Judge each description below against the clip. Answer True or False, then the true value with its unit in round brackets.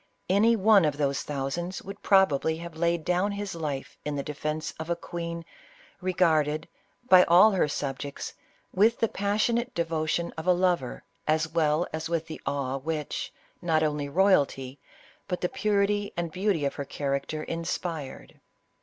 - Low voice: False (165 Hz)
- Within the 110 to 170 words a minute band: True (165 wpm)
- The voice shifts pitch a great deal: False (3.8 semitones)